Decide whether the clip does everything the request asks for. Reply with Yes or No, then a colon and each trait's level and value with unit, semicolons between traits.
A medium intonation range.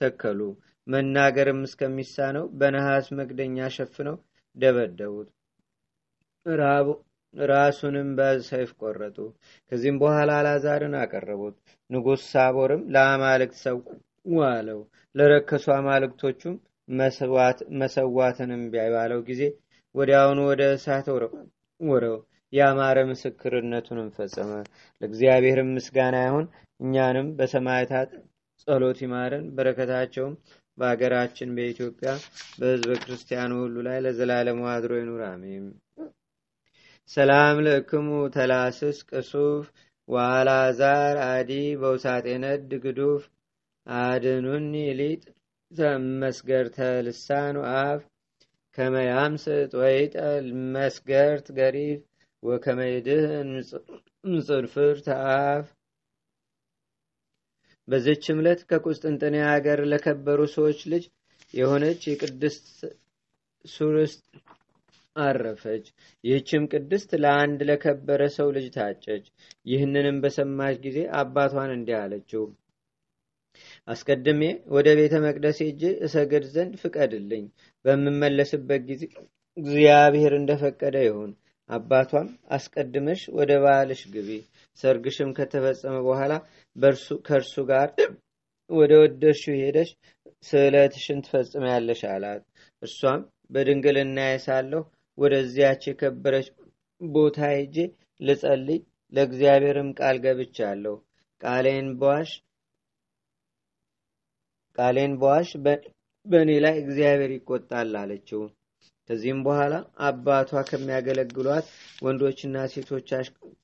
No: narrow, 2.2 semitones